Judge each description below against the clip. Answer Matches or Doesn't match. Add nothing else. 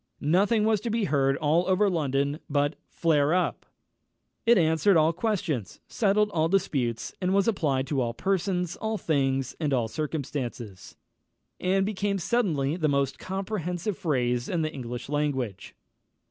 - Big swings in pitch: Matches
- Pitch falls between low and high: Matches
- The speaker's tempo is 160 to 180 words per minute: Doesn't match